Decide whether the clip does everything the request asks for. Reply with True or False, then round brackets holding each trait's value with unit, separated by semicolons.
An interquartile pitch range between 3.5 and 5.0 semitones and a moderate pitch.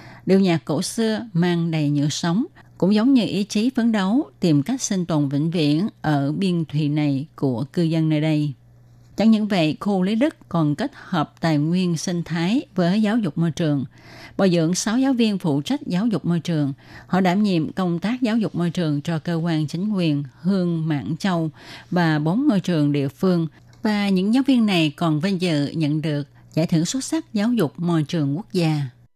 True (4.7 semitones; 170 Hz)